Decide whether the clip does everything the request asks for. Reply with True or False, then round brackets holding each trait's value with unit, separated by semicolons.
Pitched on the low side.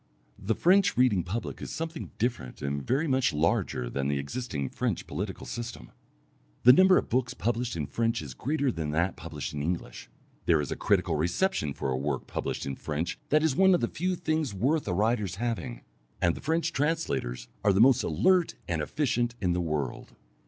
True (110 Hz)